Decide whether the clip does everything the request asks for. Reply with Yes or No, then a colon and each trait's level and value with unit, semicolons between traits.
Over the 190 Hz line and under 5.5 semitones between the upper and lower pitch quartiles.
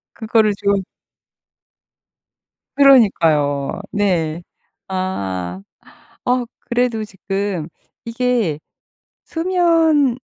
No: high, 205 Hz; wide, 6.8 semitones